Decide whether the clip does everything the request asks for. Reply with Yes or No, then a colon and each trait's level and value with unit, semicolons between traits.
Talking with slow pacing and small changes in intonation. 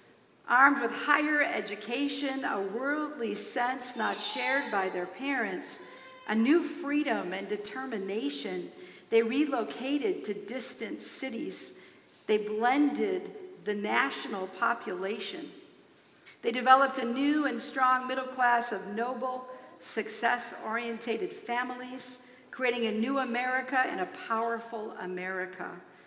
No: slow, 110 wpm; average, 3.6 semitones